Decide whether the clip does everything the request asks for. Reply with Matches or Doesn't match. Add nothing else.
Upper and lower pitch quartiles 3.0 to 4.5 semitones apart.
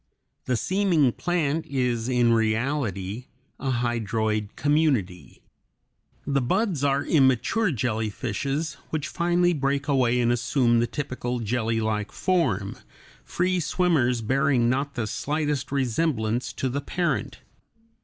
Matches